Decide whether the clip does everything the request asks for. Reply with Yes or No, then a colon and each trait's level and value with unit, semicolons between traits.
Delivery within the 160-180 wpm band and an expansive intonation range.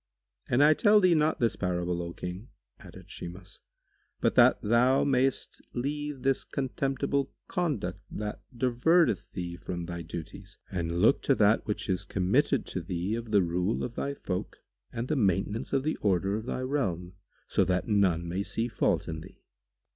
Yes: average, 170 wpm; wide, 7.0 semitones